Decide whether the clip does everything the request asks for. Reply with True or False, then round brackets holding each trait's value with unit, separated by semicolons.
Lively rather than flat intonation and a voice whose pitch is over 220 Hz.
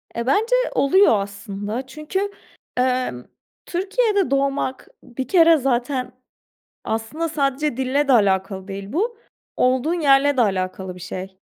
True (7.0 semitones; 260 Hz)